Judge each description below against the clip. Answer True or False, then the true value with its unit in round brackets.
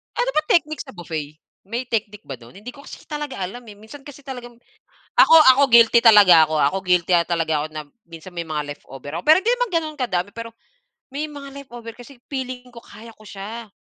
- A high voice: True (230 Hz)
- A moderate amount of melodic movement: False (7.2 semitones)